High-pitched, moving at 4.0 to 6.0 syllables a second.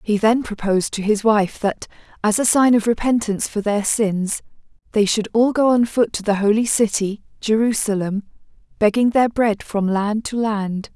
Yes: high, 215 Hz; 4.8 syllables/s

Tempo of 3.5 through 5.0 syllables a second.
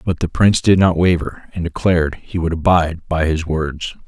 No: 5.2 syllables/s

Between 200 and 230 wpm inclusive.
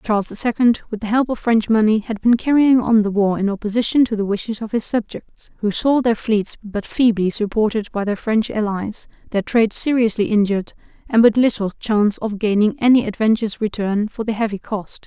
Yes: fast, 205 wpm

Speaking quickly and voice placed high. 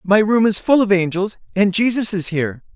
Yes: fast, 220 wpm; high, 200 Hz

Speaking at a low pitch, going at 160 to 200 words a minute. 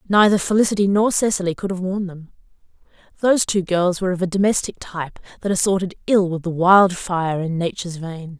No: medium, 185 Hz; average, 180 wpm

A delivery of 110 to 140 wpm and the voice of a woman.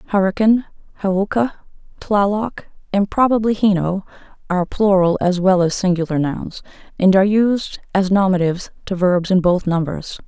Yes: slow, 135 wpm; female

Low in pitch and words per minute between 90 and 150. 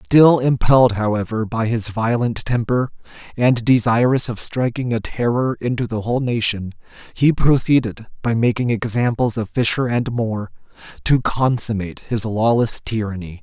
Yes: low, 115 Hz; average, 140 wpm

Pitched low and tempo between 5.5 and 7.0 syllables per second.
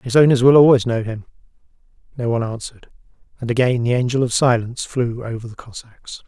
Yes: low, 120 Hz; 6.3 syllables/s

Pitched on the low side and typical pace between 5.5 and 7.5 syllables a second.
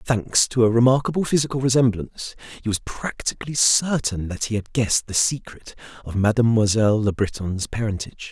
Yes: low, 115 Hz; 5.7 syllables/s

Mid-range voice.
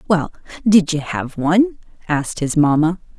Yes: medium, 170 Hz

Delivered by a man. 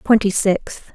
No: female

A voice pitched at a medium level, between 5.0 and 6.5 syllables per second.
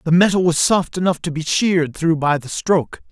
Yes: medium, 165 Hz; 5.5 syllables/s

